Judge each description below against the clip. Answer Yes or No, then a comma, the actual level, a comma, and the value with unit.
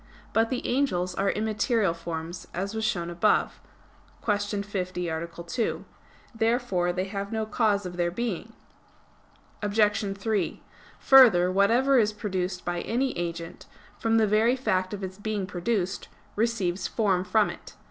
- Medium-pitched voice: No, high, 200 Hz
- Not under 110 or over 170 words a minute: Yes, average, 145 wpm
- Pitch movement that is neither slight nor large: Yes, average, 3.7 semitones